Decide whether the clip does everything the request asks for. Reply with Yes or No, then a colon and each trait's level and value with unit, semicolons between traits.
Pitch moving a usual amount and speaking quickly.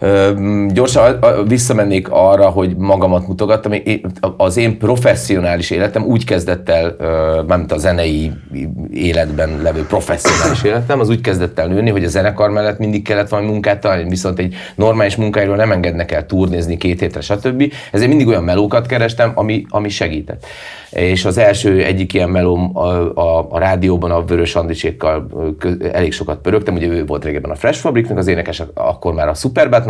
Yes: average, 3.5 semitones; fast, 170 wpm